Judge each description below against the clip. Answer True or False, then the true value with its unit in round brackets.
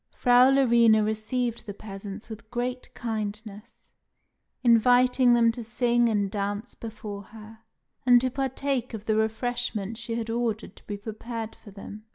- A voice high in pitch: True (225 Hz)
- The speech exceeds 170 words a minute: False (150 wpm)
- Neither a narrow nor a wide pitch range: False (2.2 semitones)